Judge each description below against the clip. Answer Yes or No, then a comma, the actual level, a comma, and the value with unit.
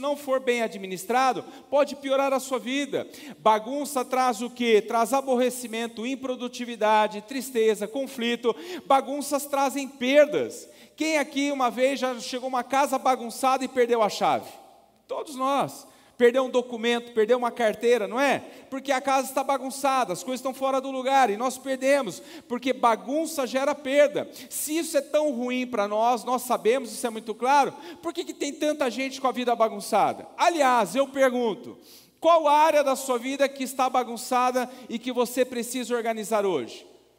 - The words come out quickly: No, average, 165 wpm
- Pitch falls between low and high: No, very high, 260 Hz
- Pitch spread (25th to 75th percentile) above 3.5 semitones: No, narrow, 2.5 semitones